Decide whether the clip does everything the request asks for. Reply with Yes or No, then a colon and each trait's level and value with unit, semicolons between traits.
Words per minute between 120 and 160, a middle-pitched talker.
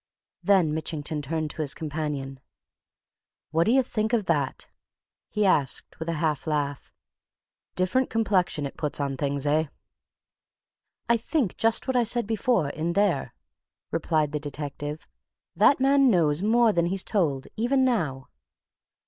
Yes: average, 140 wpm; medium, 165 Hz